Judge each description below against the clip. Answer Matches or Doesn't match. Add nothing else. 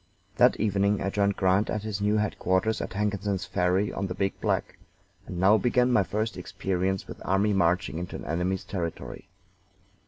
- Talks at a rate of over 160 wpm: Matches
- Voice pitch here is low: Matches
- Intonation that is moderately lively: Doesn't match